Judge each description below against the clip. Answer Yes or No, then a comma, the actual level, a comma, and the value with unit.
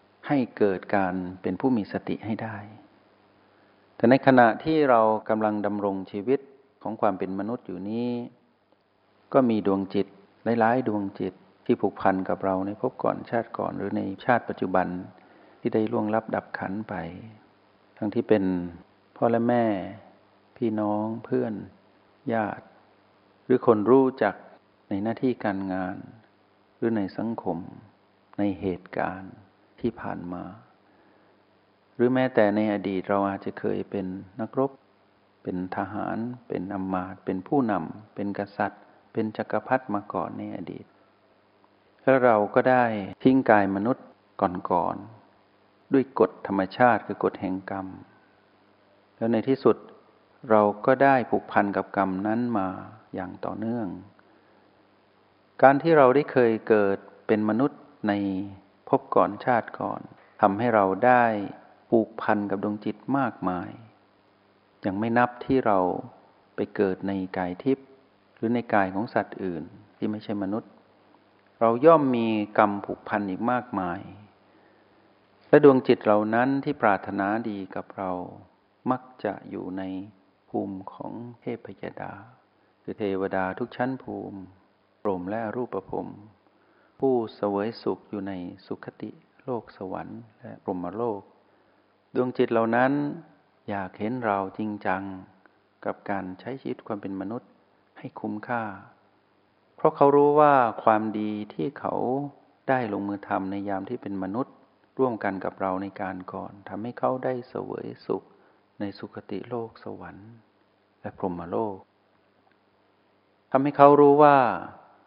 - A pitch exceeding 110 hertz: No, low, 105 Hz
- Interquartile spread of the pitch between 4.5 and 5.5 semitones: No, average, 3.2 semitones